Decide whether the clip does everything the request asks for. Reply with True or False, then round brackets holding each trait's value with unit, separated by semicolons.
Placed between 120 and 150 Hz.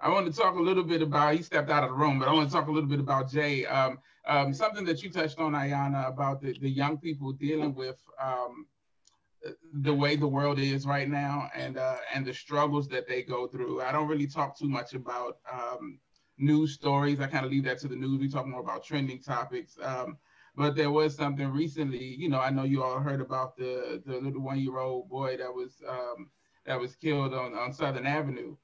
True (140 Hz)